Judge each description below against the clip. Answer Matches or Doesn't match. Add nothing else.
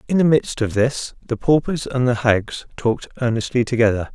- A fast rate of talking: Doesn't match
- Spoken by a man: Matches